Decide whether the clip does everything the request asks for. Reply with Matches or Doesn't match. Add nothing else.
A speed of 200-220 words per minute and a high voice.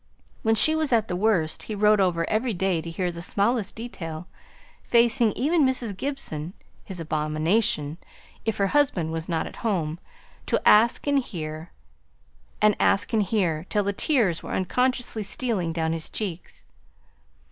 Doesn't match